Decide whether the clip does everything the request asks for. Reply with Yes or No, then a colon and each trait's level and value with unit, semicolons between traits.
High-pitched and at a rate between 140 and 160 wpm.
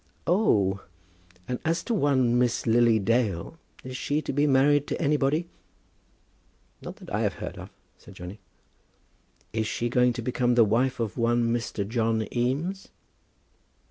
No: low, 125 Hz; average, 155 wpm